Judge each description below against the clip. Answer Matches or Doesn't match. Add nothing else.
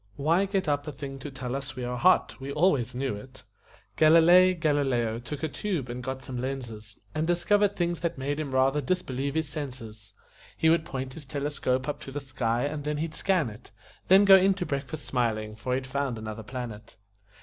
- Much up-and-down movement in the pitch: Doesn't match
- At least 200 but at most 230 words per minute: Matches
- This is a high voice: Doesn't match